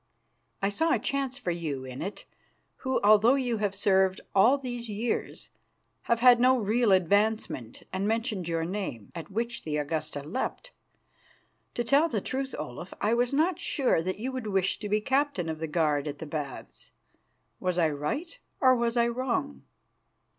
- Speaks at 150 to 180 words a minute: Yes, average, 175 wpm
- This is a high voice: Yes, high, 210 Hz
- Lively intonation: Yes, wide, 6.9 semitones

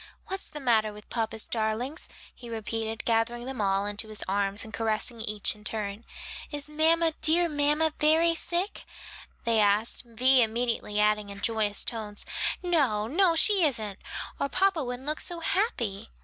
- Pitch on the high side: Yes, high, 230 Hz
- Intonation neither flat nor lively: No, wide, 6.2 semitones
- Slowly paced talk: No, average, 160 wpm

